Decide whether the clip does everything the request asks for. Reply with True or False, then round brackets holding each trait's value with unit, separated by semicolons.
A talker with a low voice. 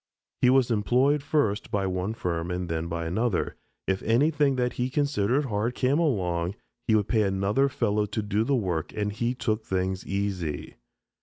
True (105 Hz)